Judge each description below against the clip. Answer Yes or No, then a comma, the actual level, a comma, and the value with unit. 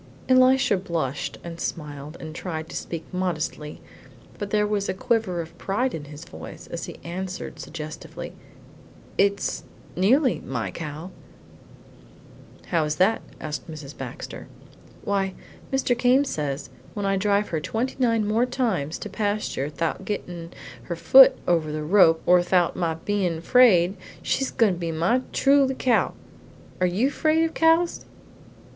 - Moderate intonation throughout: No, wide, 5.9 semitones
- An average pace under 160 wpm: Yes, average, 150 wpm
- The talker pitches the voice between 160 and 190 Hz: Yes, medium, 185 Hz